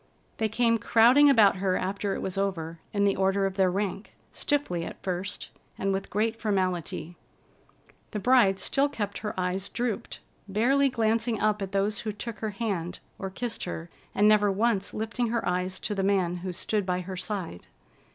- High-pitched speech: Yes, high, 200 Hz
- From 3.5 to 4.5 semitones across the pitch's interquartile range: No, average, 3.0 semitones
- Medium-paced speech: Yes, average, 180 wpm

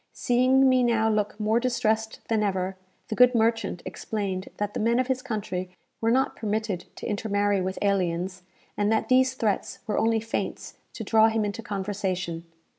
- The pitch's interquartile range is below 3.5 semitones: Yes, narrow, 2.5 semitones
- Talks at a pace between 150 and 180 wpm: Yes, average, 175 wpm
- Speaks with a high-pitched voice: Yes, high, 215 Hz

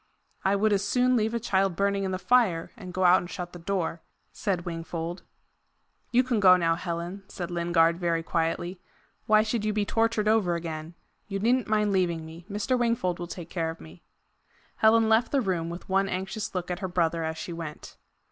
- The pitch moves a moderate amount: Yes, average, 3.9 semitones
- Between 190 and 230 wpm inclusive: Yes, fast, 205 wpm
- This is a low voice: No, medium, 185 Hz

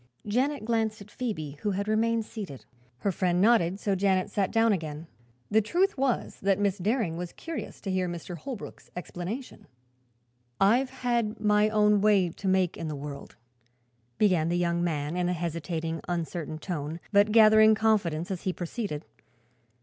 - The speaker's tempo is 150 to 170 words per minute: Yes, average, 165 wpm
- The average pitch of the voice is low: No, high, 195 Hz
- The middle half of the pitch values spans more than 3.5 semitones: Yes, average, 4.0 semitones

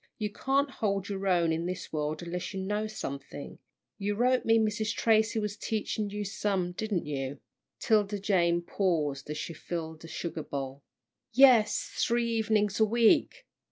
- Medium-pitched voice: No, high, 200 Hz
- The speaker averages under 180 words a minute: Yes, average, 160 wpm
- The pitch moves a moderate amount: Yes, average, 4.3 semitones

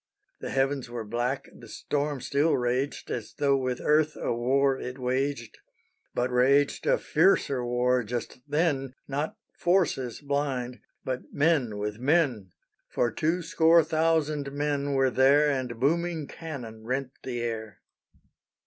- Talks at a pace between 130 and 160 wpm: Yes, average, 140 wpm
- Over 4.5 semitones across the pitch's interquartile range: No, average, 3.2 semitones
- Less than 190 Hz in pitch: Yes, low, 135 Hz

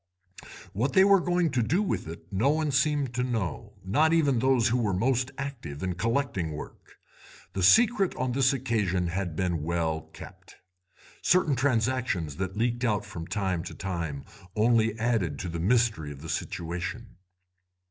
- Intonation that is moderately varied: No, wide, 6.9 semitones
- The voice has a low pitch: Yes, low, 115 Hz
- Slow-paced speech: No, average, 165 wpm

